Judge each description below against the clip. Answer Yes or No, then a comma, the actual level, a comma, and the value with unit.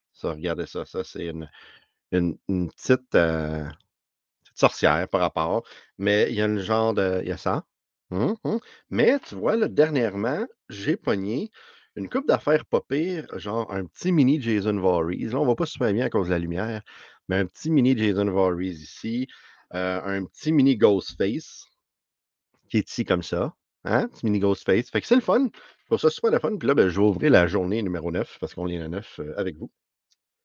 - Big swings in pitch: No, average, 4.7 semitones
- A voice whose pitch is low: Yes, low, 100 Hz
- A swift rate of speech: No, average, 205 wpm